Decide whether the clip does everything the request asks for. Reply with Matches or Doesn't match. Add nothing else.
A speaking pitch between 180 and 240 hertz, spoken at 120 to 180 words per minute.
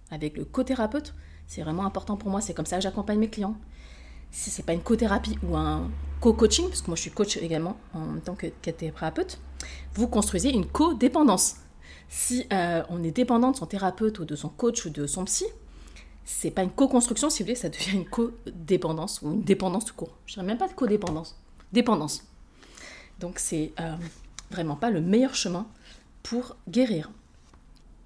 Doesn't match